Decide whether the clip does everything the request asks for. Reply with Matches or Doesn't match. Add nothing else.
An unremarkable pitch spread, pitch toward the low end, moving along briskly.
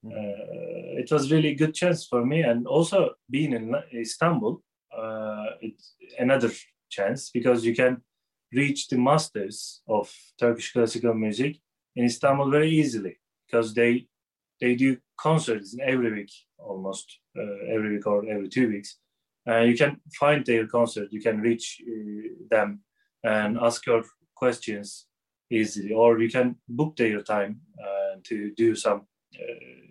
Matches